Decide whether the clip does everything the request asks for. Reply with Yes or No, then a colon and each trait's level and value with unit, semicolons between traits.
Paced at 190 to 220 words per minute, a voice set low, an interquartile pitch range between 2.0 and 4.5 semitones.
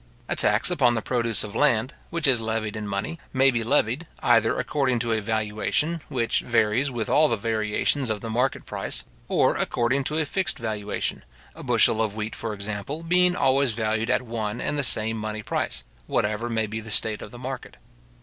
Yes: average, 195 wpm; low, 115 Hz; average, 3.7 semitones